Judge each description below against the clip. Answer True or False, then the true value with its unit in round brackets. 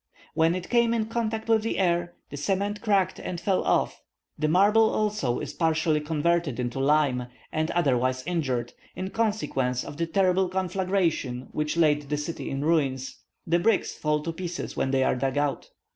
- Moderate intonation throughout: True (4.9 semitones)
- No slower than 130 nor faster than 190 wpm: True (175 wpm)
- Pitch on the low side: False (165 Hz)